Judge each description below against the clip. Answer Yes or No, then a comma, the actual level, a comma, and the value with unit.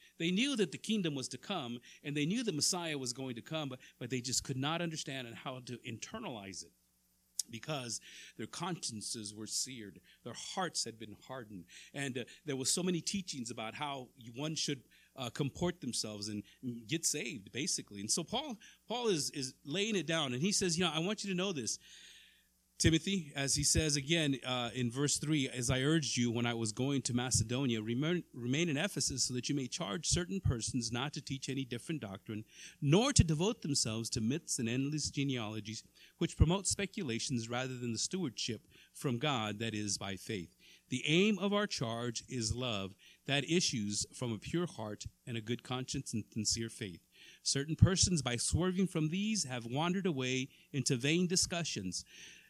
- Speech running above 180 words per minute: Yes, average, 190 wpm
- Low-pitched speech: Yes, low, 130 Hz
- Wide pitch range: Yes, wide, 5.7 semitones